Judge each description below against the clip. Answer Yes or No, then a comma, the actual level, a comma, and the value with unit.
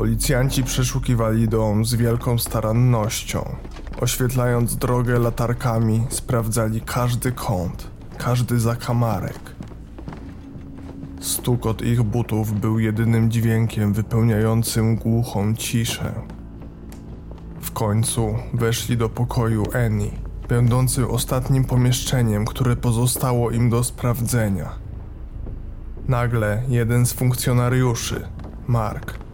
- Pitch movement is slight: Yes, narrow, 1.8 semitones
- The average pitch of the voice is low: Yes, low, 115 Hz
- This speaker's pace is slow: Yes, slow, 90 wpm